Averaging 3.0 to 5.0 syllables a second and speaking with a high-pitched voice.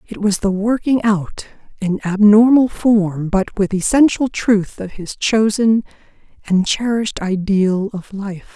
Yes: 4.0 syllables/s; high, 205 Hz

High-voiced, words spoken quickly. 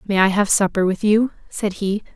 Yes: high, 200 Hz; fast, 220 wpm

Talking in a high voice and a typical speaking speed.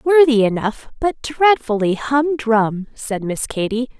No: high, 245 Hz; slow, 120 wpm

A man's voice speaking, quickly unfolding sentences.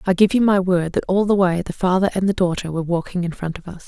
No: female; fast, 310 wpm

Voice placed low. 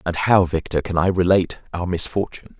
Yes: very low, 90 Hz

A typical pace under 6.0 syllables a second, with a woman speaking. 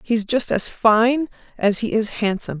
Yes: 4.5 syllables/s; female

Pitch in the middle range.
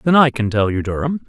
No: low, 125 Hz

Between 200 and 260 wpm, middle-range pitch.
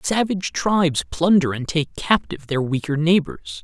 No: average, 150 wpm; medium, 155 Hz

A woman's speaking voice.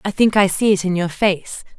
Yes: female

